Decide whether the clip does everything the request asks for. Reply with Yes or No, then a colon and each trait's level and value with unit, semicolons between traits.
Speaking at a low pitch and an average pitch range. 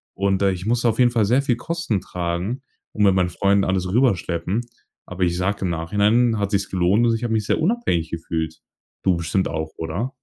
Yes: low, 100 Hz; average, 4.8 semitones